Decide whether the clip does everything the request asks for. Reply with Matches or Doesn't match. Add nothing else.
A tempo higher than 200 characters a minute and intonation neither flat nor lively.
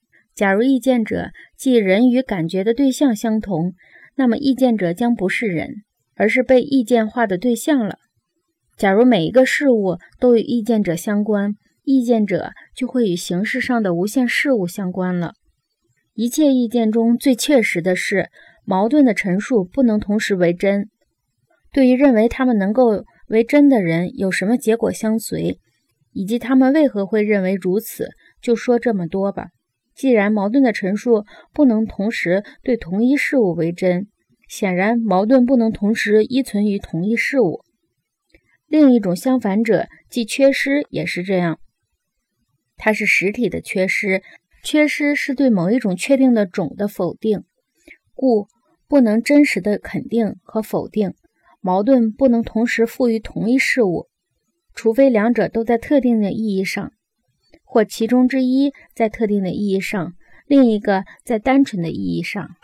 Matches